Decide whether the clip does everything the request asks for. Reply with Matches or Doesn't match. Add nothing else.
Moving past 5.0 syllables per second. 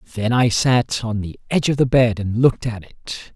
Matches